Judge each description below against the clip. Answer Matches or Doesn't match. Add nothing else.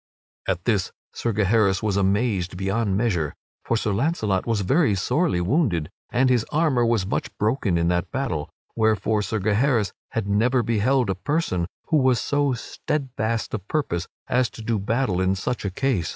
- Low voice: Matches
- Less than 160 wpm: Doesn't match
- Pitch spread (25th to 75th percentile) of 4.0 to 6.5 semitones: Matches